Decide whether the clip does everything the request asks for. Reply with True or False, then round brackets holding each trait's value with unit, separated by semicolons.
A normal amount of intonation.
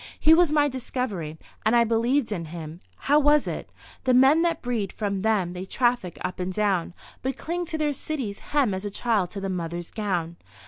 False (6.8 semitones)